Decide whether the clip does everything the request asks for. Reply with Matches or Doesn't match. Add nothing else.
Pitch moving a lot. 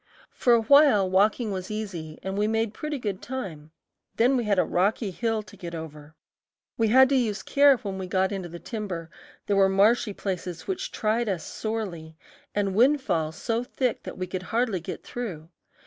Doesn't match